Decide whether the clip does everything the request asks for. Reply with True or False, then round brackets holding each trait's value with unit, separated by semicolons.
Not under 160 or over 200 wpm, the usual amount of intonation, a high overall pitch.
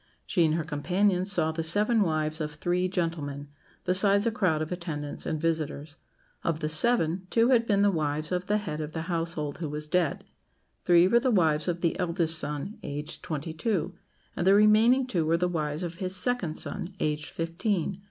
False (195 wpm; 3.8 semitones; 170 Hz)